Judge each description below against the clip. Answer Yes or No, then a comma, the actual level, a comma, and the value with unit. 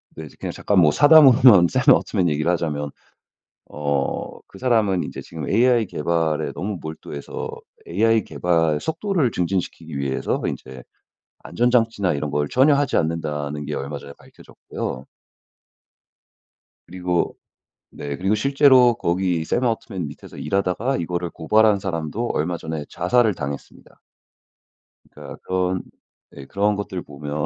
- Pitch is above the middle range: No, very low, 90 Hz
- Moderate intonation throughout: No, wide, 6.6 semitones